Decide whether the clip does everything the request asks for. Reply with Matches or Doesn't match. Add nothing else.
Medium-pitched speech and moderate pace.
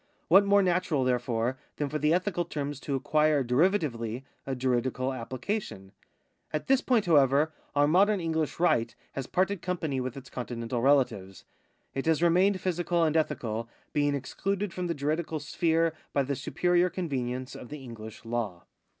Matches